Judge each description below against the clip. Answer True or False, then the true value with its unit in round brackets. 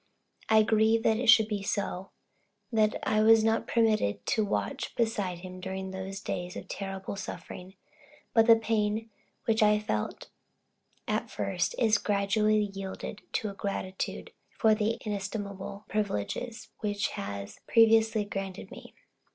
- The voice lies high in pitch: True (210 Hz)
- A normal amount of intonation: False (2.3 semitones)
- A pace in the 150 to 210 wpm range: False (140 wpm)